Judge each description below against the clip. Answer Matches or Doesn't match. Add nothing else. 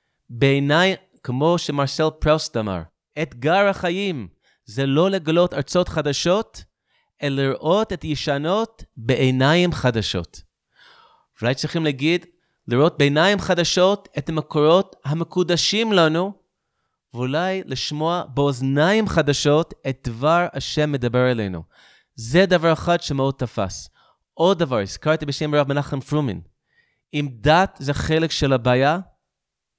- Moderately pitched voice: Matches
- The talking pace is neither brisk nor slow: Matches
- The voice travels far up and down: Doesn't match